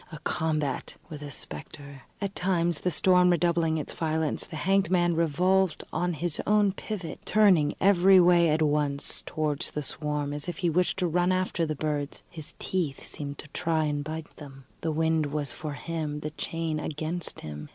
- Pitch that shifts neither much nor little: Yes, average, 3.0 semitones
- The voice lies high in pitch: No, medium, 160 Hz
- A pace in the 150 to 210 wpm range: Yes, average, 185 wpm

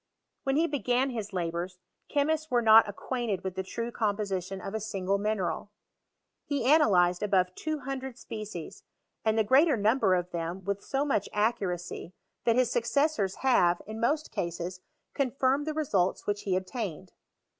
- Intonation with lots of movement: Yes, wide, 5.8 semitones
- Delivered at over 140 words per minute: Yes, average, 155 wpm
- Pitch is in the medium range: No, high, 215 Hz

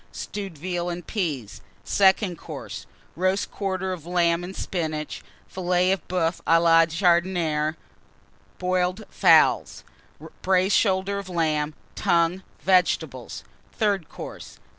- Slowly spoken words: Yes, slow, 115 wpm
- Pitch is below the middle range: No, medium, 180 Hz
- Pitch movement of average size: No, narrow, 2.3 semitones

